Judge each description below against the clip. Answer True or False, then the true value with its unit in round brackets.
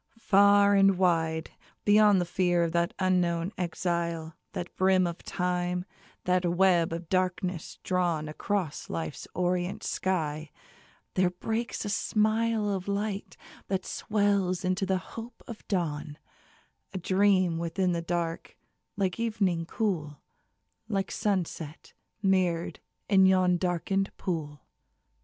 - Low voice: False (185 Hz)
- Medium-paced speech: False (120 wpm)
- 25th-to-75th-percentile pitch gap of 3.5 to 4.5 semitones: False (2.5 semitones)